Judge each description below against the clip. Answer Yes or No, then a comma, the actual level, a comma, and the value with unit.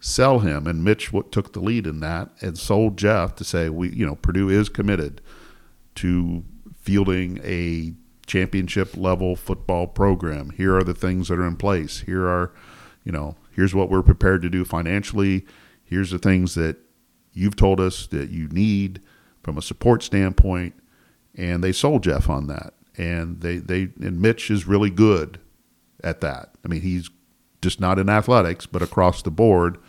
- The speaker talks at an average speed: Yes, average, 175 wpm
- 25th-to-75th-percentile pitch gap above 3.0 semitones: No, narrow, 2.6 semitones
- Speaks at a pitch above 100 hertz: No, very low, 95 Hz